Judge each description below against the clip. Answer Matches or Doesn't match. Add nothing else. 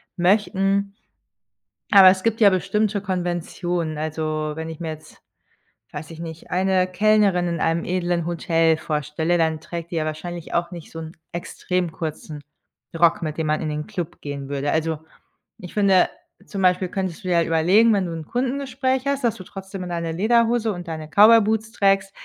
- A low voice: Doesn't match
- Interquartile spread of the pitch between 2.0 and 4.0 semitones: Matches